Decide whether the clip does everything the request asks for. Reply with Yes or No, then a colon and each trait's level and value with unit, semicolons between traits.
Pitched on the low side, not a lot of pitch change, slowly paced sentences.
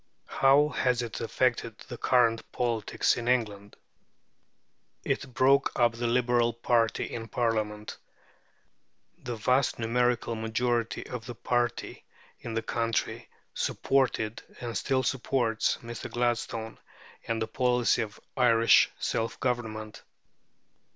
Yes: low, 120 Hz; narrow, 1.5 semitones; slow, 115 wpm